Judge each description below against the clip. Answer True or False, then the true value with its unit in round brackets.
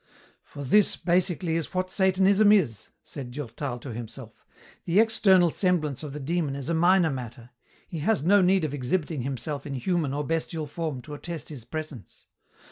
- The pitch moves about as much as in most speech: True (4.9 semitones)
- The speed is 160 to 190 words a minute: True (175 wpm)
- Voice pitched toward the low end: False (155 Hz)